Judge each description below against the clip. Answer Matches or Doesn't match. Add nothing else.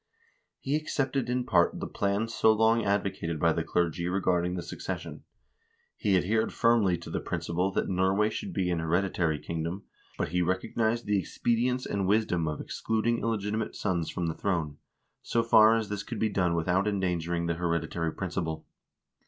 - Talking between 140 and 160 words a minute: Doesn't match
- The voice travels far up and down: Doesn't match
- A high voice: Doesn't match